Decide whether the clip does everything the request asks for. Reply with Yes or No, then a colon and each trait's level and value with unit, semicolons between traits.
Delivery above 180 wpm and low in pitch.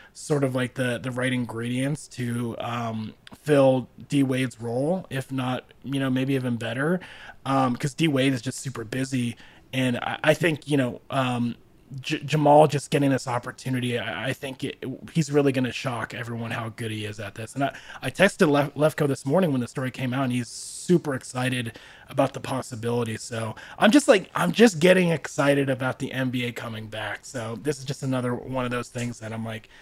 Yes: fast, 205 wpm; low, 130 Hz